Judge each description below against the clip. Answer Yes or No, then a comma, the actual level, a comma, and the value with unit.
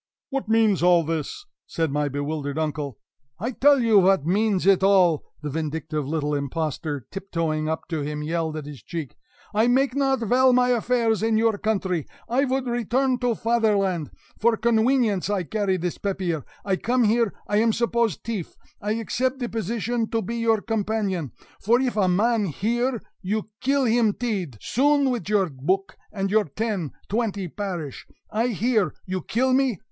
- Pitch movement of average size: No, wide, 6.0 semitones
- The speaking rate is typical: Yes, average, 170 wpm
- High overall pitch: Yes, high, 210 Hz